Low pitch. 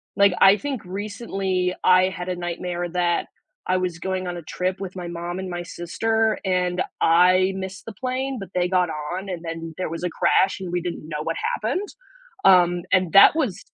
No: medium, 185 Hz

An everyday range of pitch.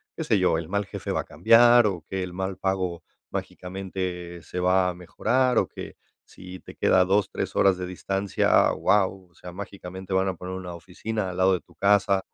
No: narrow, 1.4 semitones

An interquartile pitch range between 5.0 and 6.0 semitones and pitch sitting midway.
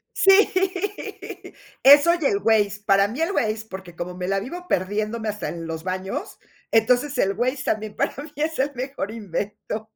No: average, 5.3 semitones; high, 215 Hz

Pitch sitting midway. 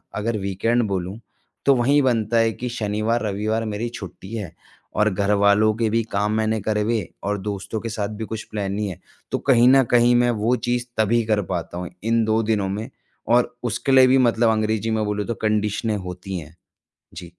No: low, 110 Hz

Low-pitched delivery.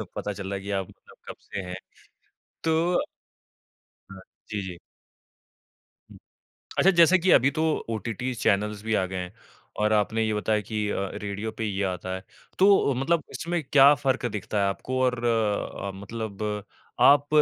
Yes: low, 110 Hz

